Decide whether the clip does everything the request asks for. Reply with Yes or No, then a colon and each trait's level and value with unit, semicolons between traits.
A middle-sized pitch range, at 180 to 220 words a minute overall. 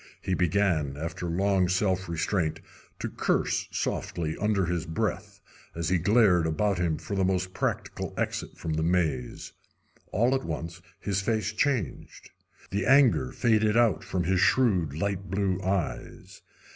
No: average, 3.5 semitones; average, 145 wpm